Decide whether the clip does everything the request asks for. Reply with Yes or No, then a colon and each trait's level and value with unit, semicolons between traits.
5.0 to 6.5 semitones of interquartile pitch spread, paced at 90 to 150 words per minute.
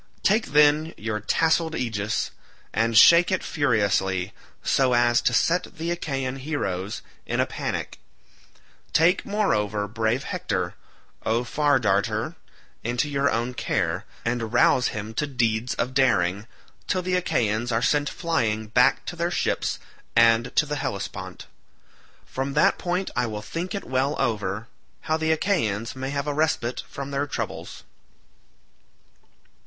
Yes: wide, 5.6 semitones; average, 140 wpm